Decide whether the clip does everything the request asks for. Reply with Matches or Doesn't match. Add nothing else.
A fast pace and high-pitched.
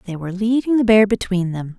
Matches